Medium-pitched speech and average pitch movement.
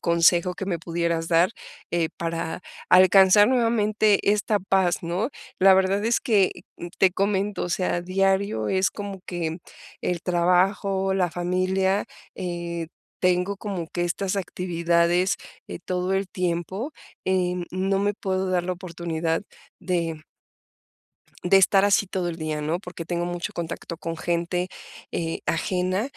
No: medium, 180 Hz; narrow, 2.2 semitones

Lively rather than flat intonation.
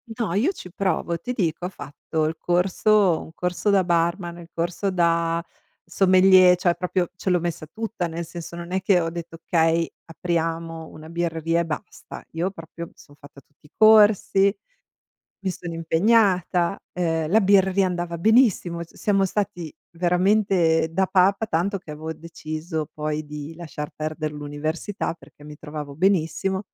No: average, 2.7 semitones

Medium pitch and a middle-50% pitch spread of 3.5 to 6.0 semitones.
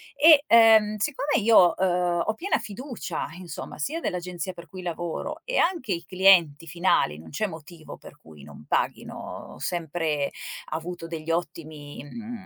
Yes: medium, 175 Hz; average, 5.2 semitones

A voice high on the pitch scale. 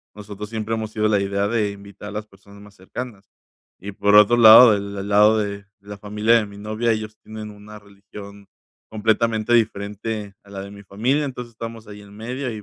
No: low, 105 Hz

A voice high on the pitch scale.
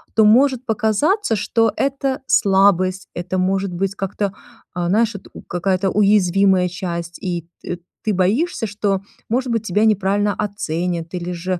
Yes: high, 195 Hz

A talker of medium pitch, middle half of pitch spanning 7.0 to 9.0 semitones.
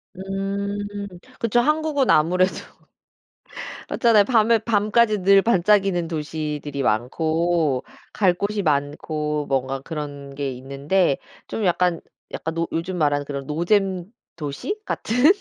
No: medium, 175 Hz; wide, 5.5 semitones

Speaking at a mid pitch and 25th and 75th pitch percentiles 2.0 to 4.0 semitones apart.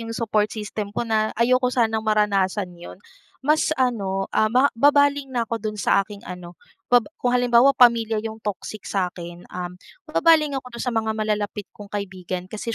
No: high, 220 Hz; average, 3.5 semitones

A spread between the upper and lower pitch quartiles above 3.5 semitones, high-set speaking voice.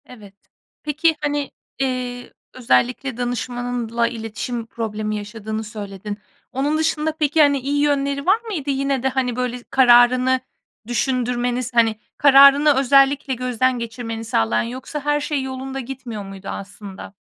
No: average, 3.2 semitones; very high, 250 Hz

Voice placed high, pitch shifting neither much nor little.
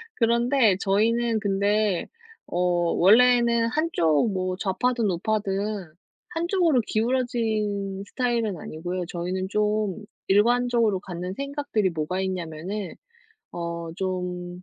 Yes: high, 205 Hz; average, 4.3 semitones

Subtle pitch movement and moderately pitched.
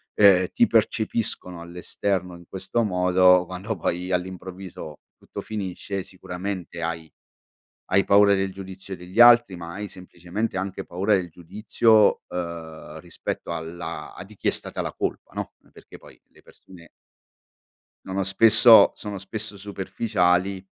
No: narrow, 2.2 semitones; very low, 95 Hz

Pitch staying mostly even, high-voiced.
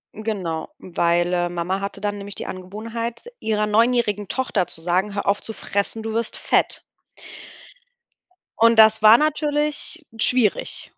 No: average, 3.3 semitones; high, 210 Hz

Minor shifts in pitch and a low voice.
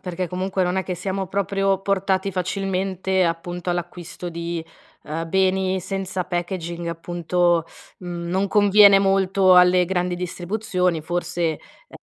No: narrow, 1.6 semitones; medium, 180 Hz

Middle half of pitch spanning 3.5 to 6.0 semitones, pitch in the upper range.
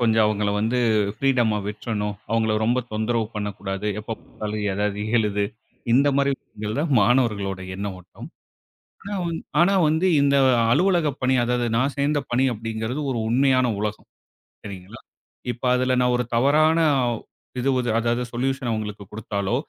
No: average, 3.9 semitones; low, 115 Hz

